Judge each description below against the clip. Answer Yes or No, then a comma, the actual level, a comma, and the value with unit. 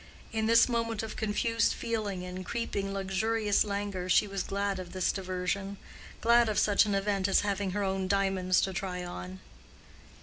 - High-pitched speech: Yes, high, 200 Hz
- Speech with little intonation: Yes, narrow, 2.2 semitones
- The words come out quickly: No, average, 165 wpm